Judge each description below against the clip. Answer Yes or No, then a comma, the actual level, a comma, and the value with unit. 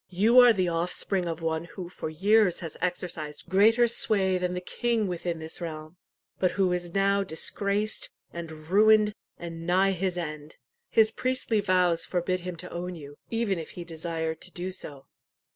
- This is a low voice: No, medium, 180 Hz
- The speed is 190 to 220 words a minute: No, average, 175 wpm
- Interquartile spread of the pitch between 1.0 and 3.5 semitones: Yes, average, 3.1 semitones